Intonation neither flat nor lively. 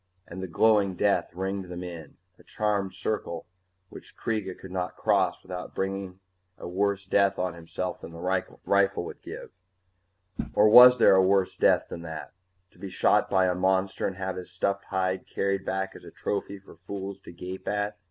No: narrow, 1.5 semitones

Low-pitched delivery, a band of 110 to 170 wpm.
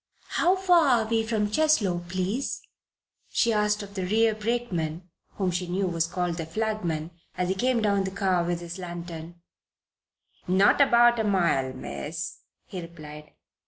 No: high, 190 Hz; average, 160 wpm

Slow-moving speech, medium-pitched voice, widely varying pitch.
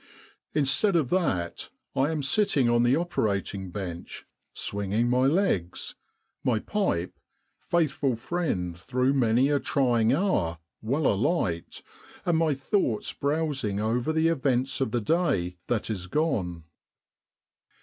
No: slow, 125 wpm; low, 130 Hz; wide, 7.4 semitones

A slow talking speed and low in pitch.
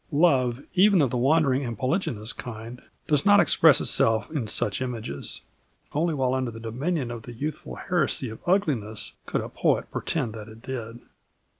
No: average, 170 wpm; low, 130 Hz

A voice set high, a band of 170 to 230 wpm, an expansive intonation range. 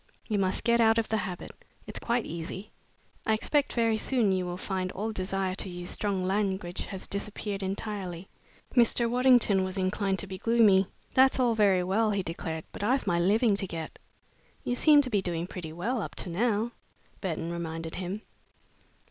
No: high, 195 Hz; average, 180 wpm; average, 3.5 semitones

